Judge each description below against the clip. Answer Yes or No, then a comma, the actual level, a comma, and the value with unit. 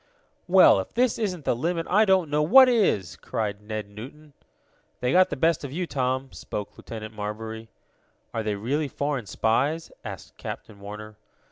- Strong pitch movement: Yes, wide, 7.4 semitones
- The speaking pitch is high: No, low, 130 Hz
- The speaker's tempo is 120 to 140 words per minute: No, average, 165 wpm